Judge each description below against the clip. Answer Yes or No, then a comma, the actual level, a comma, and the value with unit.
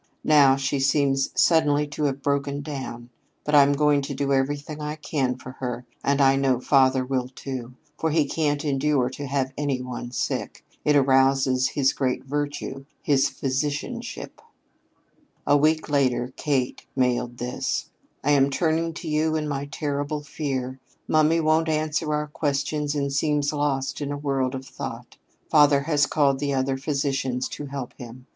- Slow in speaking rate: No, average, 165 wpm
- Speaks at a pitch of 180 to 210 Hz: No, medium, 140 Hz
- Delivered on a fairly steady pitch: Yes, narrow, 1.9 semitones